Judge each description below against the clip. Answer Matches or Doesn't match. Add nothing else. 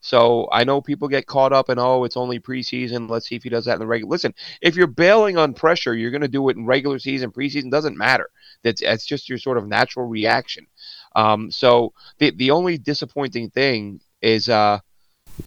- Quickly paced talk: Matches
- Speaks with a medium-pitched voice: Doesn't match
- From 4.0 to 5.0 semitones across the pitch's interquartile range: Doesn't match